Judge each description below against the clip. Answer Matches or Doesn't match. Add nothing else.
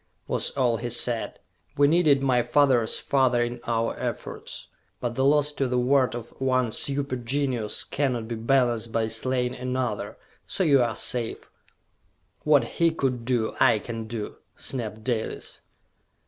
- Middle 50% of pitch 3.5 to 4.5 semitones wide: Doesn't match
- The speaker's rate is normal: Matches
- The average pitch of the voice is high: Doesn't match